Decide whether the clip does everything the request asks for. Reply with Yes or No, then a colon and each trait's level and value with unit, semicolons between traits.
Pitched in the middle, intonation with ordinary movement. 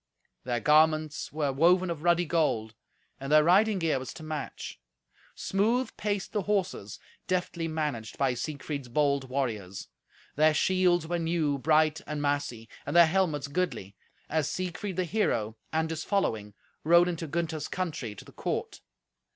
Yes: medium, 155 Hz; average, 3.8 semitones